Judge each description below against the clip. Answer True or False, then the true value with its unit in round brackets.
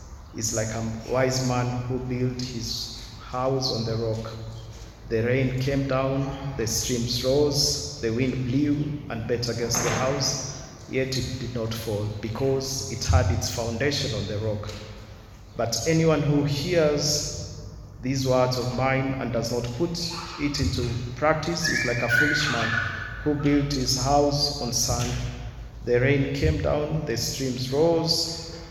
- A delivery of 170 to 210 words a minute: False (155 wpm)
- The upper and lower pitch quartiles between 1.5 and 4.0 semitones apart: True (3.2 semitones)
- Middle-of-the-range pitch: False (125 Hz)